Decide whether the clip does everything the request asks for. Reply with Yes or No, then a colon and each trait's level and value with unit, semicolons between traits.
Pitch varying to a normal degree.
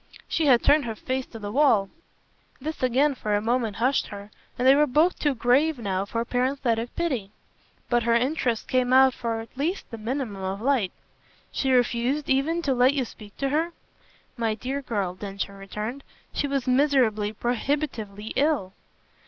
Yes: average, 4.2 semitones